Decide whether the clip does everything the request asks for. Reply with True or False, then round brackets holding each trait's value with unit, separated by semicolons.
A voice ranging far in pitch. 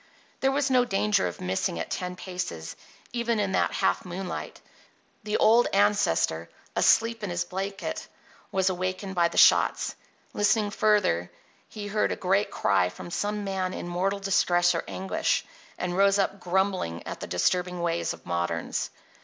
False (2.8 semitones)